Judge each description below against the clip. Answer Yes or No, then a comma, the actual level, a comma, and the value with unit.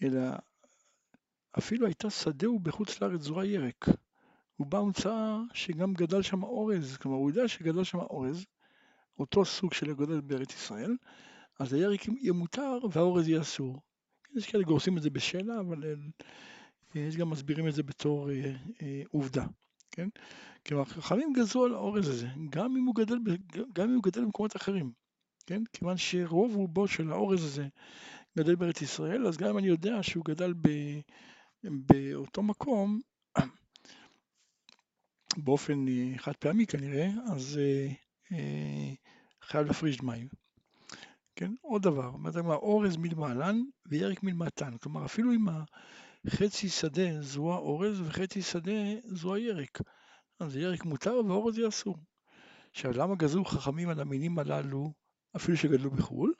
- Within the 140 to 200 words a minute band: Yes, average, 145 wpm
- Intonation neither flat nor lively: No, wide, 5.9 semitones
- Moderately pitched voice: Yes, medium, 175 Hz